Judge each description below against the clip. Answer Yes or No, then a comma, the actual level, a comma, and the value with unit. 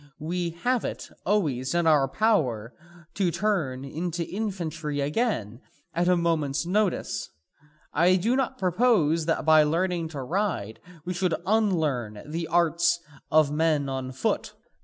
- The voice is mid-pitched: Yes, medium, 165 Hz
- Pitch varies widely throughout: No, average, 4.2 semitones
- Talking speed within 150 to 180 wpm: No, average, 140 wpm